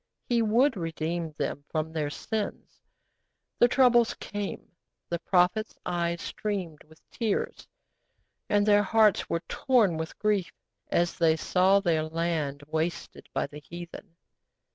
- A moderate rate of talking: No, slow, 130 wpm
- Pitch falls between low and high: Yes, medium, 175 Hz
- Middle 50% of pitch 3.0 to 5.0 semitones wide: Yes, average, 4.6 semitones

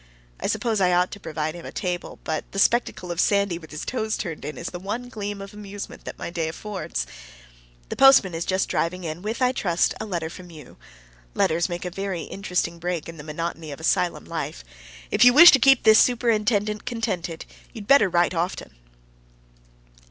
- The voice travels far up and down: No, average, 4.2 semitones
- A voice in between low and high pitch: Yes, medium, 180 Hz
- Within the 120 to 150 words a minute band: No, average, 195 wpm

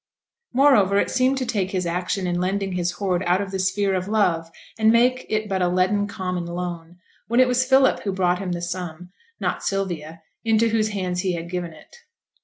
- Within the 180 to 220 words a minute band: Yes, fast, 205 wpm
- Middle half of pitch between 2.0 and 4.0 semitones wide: Yes, average, 3.2 semitones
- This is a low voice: No, high, 190 Hz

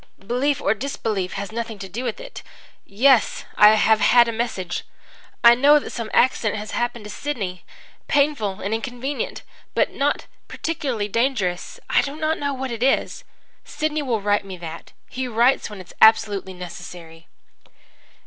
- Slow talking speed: No, average, 165 wpm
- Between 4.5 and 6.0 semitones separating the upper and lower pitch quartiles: Yes, average, 5.0 semitones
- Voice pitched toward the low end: No, high, 230 Hz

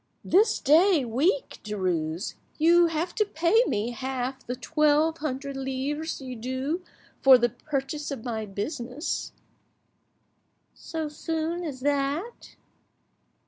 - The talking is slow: Yes, slow, 110 wpm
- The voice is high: Yes, very high, 280 Hz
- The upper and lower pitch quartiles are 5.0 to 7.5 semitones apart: No, average, 4.3 semitones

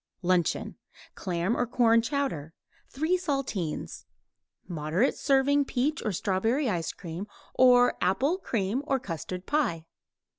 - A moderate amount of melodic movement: No, wide, 7.3 semitones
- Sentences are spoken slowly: Yes, slow, 115 wpm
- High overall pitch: Yes, high, 230 Hz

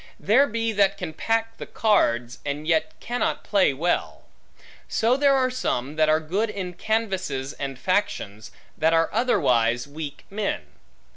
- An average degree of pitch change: No, wide, 7.7 semitones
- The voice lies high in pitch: No, medium, 180 Hz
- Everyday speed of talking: Yes, average, 150 wpm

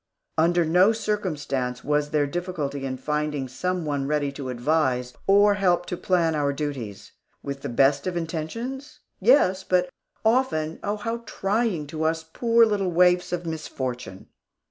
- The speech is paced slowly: No, average, 150 wpm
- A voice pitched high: No, medium, 160 Hz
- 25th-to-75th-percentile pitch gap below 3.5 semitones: No, average, 4.8 semitones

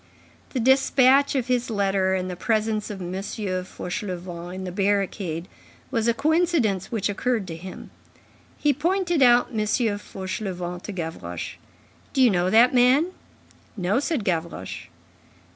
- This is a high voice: Yes, high, 205 Hz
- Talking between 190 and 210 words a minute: No, average, 140 wpm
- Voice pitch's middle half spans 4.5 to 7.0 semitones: Yes, average, 5.3 semitones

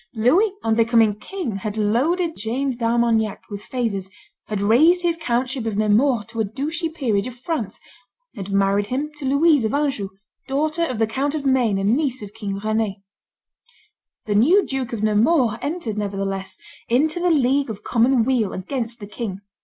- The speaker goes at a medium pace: Yes, average, 170 wpm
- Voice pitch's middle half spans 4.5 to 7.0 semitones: Yes, average, 5.1 semitones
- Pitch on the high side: Yes, high, 235 Hz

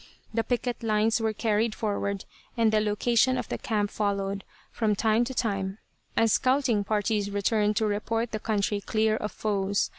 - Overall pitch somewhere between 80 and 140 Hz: No, high, 215 Hz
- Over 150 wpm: Yes, average, 170 wpm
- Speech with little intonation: Yes, narrow, 1.8 semitones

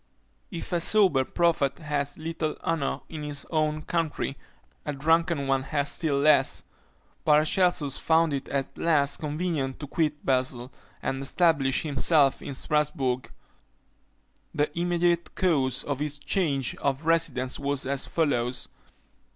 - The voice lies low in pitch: No, medium, 150 Hz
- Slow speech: Yes, slow, 130 wpm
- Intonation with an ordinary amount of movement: Yes, average, 3.1 semitones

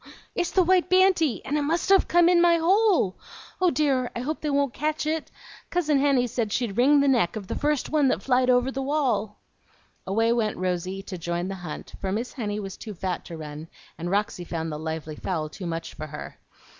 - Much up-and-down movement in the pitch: Yes, wide, 8.5 semitones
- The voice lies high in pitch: Yes, high, 245 Hz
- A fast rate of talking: Yes, fast, 220 wpm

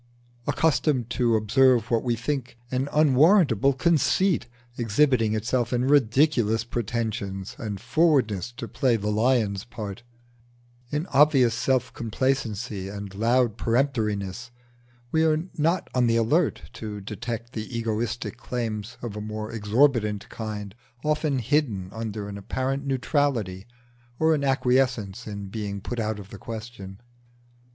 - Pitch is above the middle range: No, low, 115 Hz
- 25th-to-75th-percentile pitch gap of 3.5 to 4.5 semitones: Yes, average, 4.0 semitones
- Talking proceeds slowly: Yes, slow, 130 wpm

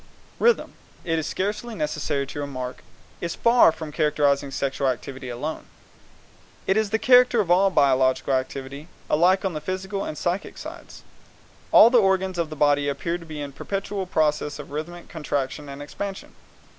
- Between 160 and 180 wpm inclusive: Yes, average, 170 wpm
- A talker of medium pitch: Yes, medium, 155 Hz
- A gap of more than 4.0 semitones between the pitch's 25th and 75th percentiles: Yes, average, 5.2 semitones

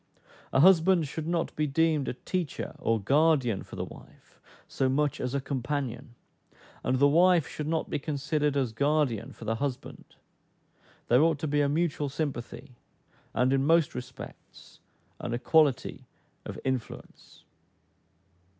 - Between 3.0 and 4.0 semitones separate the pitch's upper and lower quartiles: Yes, average, 3.5 semitones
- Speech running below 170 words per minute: Yes, average, 145 wpm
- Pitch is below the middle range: No, medium, 145 Hz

